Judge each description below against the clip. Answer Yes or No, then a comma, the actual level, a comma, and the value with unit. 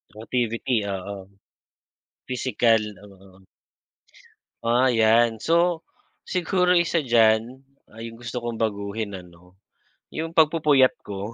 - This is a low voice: Yes, low, 115 Hz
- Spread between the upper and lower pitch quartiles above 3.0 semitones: Yes, average, 3.9 semitones